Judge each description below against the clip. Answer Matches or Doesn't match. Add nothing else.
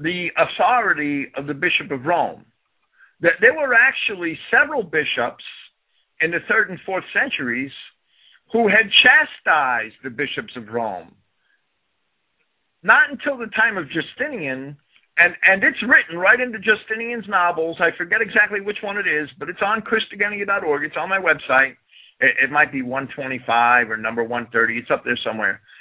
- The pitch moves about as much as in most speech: Doesn't match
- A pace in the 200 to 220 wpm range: Doesn't match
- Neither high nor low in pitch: Matches